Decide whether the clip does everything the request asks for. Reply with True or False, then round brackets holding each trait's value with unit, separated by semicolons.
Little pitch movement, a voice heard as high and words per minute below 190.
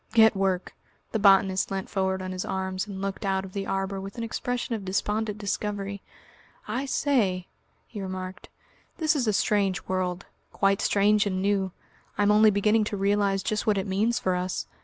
True (1.9 semitones; 195 Hz; 180 wpm)